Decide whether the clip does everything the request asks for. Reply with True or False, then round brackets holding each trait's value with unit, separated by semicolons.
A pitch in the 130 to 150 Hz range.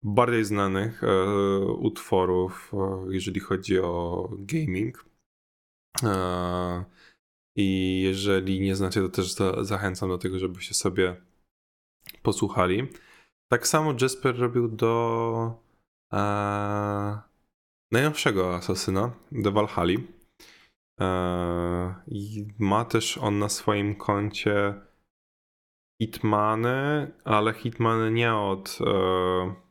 False (100 Hz)